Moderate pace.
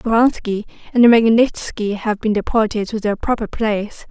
Yes: average, 145 wpm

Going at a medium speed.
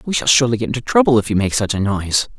No: fast, 300 wpm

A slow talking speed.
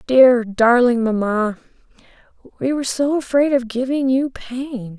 Yes: slow, 130 wpm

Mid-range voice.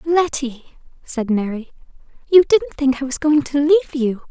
No: very high, 275 Hz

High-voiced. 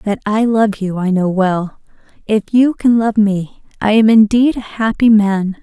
Yes: high, 210 Hz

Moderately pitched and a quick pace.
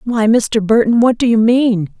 No: high, 225 Hz; fast, 210 wpm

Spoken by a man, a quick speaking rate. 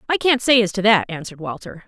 No: female; fast, 255 wpm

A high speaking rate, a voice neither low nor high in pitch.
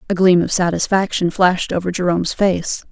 No: average, 165 wpm; medium, 180 Hz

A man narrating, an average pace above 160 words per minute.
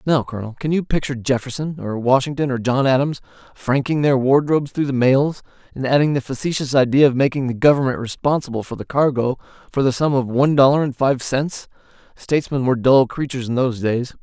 Yes: male; average, 195 wpm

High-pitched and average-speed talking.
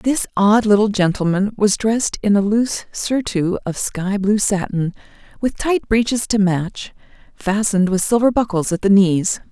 Yes: high, 205 Hz; average, 165 wpm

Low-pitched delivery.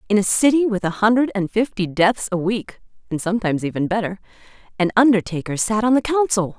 No: high, 205 Hz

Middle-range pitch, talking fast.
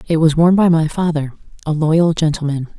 No: medium, 160 Hz; average, 195 wpm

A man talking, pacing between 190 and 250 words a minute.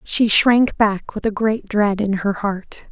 No: female; fast, 205 wpm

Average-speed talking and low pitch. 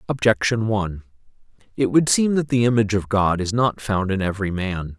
Yes: average, 195 wpm; low, 105 Hz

